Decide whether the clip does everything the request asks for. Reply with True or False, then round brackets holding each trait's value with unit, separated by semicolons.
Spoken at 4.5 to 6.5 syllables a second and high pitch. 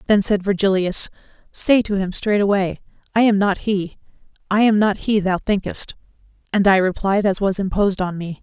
True (5.0 syllables/s; 200 Hz)